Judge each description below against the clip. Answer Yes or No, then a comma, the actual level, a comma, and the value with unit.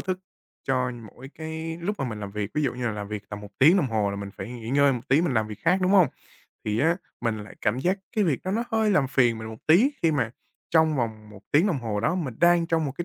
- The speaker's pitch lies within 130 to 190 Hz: Yes, low, 135 Hz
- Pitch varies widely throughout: Yes, wide, 7.1 semitones